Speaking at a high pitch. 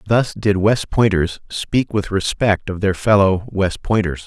No: low, 100 Hz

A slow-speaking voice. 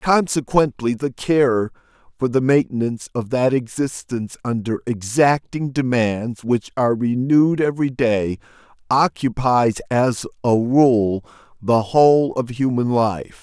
Yes: slow, 115 wpm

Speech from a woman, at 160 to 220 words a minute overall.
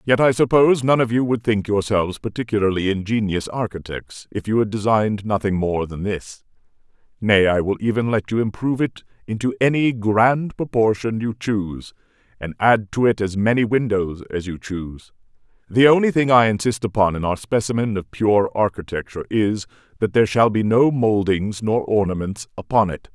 No: male; average, 175 wpm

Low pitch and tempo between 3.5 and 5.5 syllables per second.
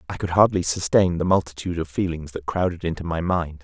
No: very low, 85 Hz; 6.1 syllables/s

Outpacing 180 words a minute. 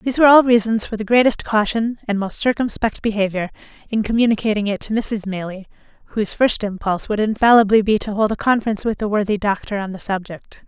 Yes: average, 195 wpm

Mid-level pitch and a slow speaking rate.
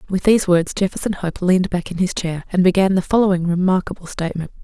No: medium, 180 Hz; fast, 205 wpm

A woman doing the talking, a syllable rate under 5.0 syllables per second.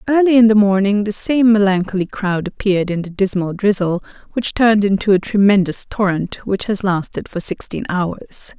No: female; 5.1 syllables/s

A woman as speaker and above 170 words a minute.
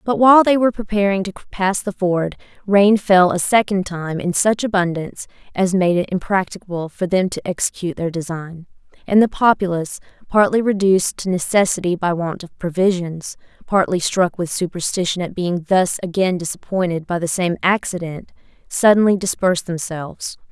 No: female; average, 160 wpm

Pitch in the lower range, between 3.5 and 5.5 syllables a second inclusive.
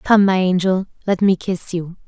No: medium, 185 Hz; 4.7 syllables/s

